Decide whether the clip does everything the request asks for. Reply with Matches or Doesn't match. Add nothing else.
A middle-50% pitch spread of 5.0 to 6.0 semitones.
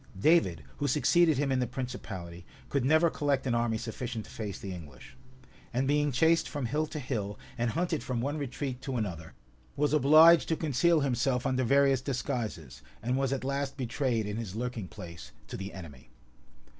Doesn't match